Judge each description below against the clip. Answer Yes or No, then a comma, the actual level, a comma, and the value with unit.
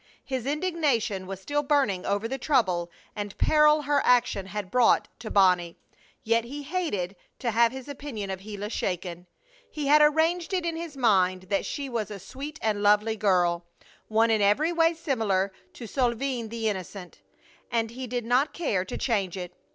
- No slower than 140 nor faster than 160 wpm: No, average, 175 wpm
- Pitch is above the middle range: Yes, high, 230 Hz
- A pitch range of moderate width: No, wide, 6.3 semitones